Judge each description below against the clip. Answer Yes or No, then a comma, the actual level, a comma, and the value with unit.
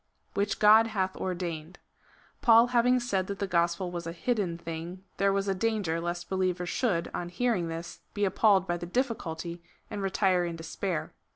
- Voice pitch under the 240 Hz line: Yes, medium, 185 Hz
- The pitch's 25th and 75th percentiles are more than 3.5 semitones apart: No, average, 3.2 semitones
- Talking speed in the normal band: Yes, average, 175 wpm